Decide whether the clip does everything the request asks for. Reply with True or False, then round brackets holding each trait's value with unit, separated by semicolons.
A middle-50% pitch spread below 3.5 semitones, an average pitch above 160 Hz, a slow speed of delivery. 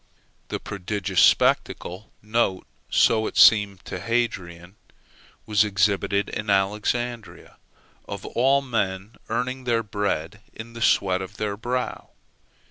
False (3.0 semitones; 105 Hz; 115 wpm)